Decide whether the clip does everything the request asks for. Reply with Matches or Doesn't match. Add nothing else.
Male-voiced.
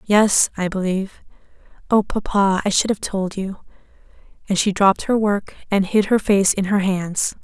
Doesn't match